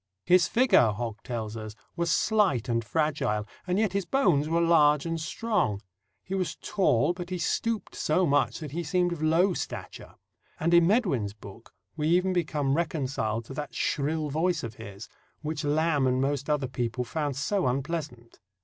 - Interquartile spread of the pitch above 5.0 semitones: Yes, wide, 5.4 semitones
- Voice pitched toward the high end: No, medium, 150 Hz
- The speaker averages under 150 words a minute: No, average, 175 wpm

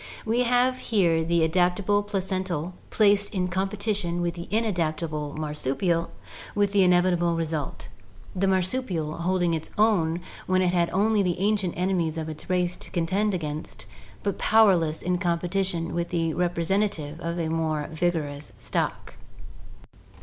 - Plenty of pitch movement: No, average, 3.1 semitones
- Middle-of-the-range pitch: Yes, medium, 175 Hz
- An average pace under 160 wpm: Yes, average, 150 wpm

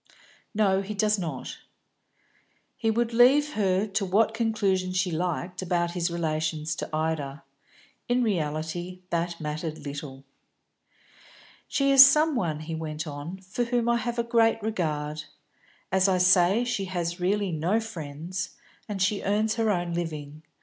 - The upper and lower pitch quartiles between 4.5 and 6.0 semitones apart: Yes, average, 5.2 semitones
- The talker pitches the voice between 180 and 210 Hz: Yes, medium, 185 Hz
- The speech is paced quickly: No, average, 150 wpm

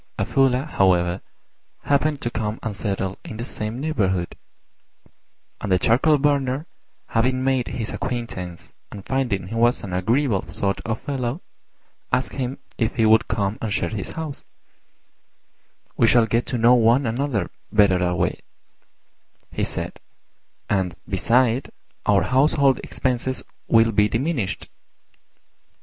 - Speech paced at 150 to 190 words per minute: No, slow, 135 wpm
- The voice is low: Yes, low, 115 Hz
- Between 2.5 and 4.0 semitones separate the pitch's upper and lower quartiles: No, average, 4.4 semitones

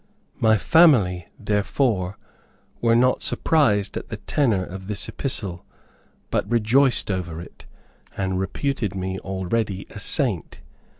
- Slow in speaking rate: Yes, slow, 120 wpm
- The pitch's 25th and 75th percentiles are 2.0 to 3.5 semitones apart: No, average, 4.2 semitones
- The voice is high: No, low, 105 Hz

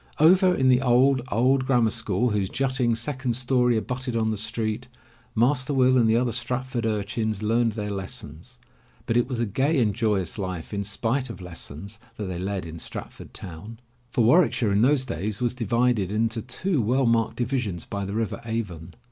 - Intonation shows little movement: No, average, 3.7 semitones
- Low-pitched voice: Yes, low, 115 Hz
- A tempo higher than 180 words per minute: Yes, average, 190 wpm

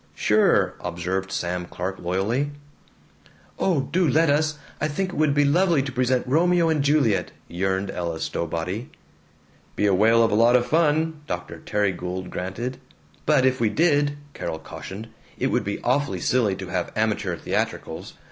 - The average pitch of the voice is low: Yes, low, 120 Hz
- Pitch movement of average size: No, wide, 7.6 semitones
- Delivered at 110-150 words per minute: No, average, 165 wpm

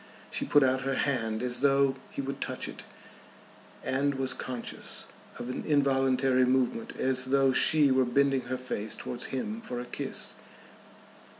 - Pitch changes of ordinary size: No, narrow, 1.5 semitones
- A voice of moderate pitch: No, low, 130 Hz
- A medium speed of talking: Yes, average, 160 wpm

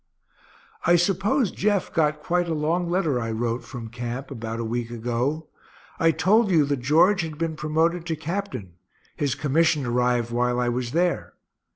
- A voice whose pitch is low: No, medium, 150 Hz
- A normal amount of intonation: No, wide, 5.8 semitones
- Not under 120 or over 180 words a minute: Yes, average, 170 wpm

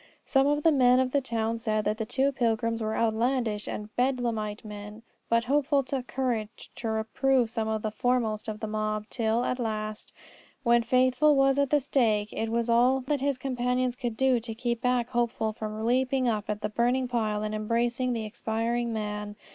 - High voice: Yes, high, 235 Hz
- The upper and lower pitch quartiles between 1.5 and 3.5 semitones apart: Yes, average, 2.7 semitones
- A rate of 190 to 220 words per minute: Yes, average, 195 wpm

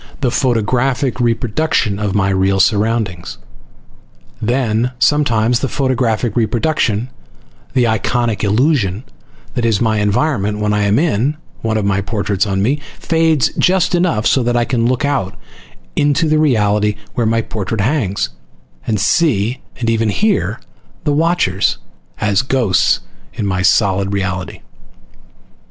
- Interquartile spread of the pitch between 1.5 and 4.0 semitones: No, average, 4.5 semitones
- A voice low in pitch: Yes, low, 115 Hz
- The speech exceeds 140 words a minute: No, slow, 135 wpm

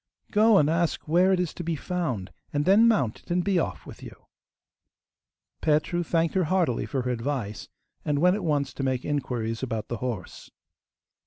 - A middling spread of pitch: No, wide, 6.1 semitones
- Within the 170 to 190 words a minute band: Yes, average, 185 wpm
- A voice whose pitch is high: No, medium, 150 Hz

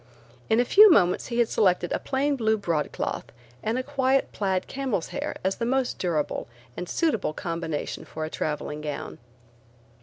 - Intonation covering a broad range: Yes, wide, 7.5 semitones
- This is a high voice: Yes, high, 210 Hz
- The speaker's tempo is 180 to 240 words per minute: No, average, 170 wpm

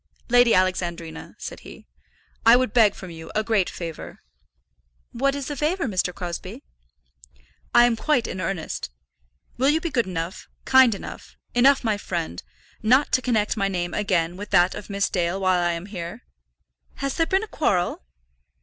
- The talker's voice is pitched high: Yes, high, 205 Hz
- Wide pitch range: Yes, wide, 6.0 semitones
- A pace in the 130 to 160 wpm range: No, average, 170 wpm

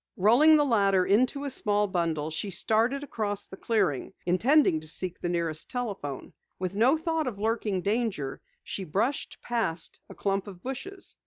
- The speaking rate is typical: Yes, average, 165 wpm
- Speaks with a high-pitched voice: Yes, high, 205 Hz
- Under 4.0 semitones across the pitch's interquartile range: No, wide, 5.5 semitones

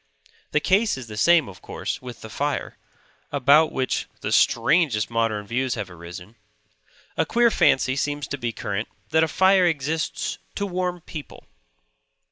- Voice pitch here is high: No, medium, 140 Hz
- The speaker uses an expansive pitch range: Yes, wide, 6.6 semitones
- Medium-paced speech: Yes, average, 155 wpm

